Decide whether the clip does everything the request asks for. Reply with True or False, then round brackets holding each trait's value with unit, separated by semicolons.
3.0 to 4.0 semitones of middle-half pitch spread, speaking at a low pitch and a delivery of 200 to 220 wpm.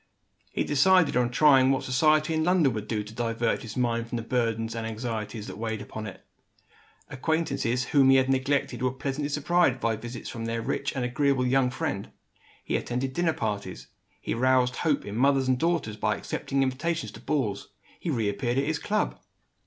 False (3.7 semitones; 130 Hz; 185 wpm)